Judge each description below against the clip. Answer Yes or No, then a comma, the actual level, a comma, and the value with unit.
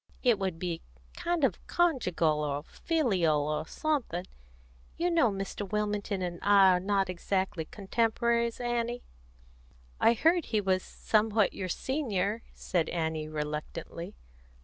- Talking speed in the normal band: No, slow, 125 wpm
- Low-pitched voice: No, high, 200 Hz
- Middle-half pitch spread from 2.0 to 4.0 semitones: No, wide, 5.4 semitones